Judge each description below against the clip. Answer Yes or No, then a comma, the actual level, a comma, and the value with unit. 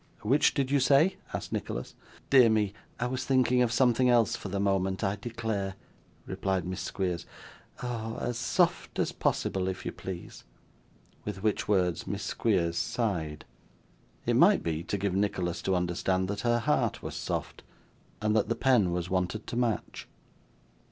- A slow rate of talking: No, average, 165 wpm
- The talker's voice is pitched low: Yes, low, 100 Hz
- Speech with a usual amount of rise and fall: Yes, average, 4.2 semitones